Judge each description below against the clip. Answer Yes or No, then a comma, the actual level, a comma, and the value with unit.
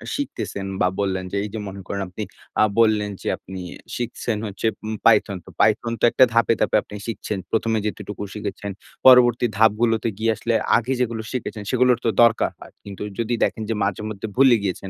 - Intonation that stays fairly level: Yes, narrow, 2.3 semitones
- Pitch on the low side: Yes, low, 110 Hz